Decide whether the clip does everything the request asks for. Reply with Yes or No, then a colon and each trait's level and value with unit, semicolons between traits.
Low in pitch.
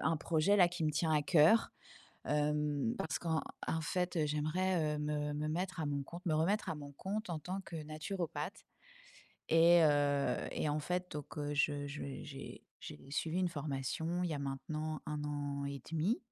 No: medium, 155 Hz